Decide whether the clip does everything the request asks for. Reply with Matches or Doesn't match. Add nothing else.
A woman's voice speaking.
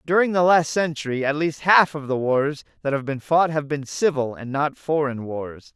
Doesn't match